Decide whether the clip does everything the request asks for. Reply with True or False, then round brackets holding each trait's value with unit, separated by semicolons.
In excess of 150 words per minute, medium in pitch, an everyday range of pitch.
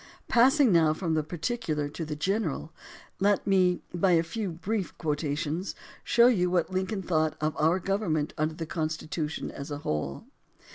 True (160 wpm; 165 Hz; 3.8 semitones)